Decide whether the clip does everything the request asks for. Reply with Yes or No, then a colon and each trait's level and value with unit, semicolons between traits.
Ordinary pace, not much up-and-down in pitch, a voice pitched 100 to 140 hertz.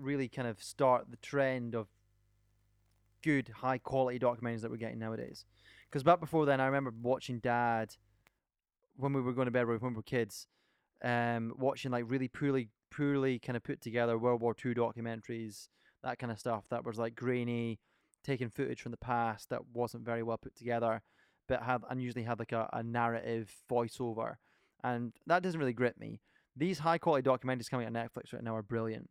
Yes: average, 190 wpm; narrow, 2.1 semitones; low, 120 Hz